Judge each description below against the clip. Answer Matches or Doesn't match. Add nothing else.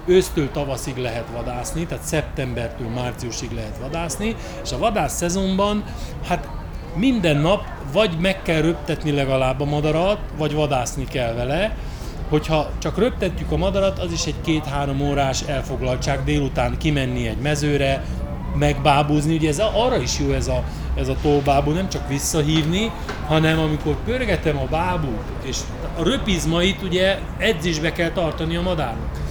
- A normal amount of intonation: Matches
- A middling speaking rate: Matches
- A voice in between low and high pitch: Matches